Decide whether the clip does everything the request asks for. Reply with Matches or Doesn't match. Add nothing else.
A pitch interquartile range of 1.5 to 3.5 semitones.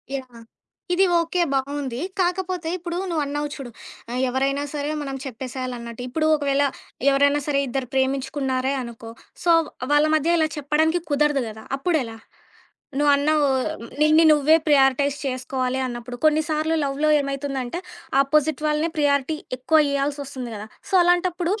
Matches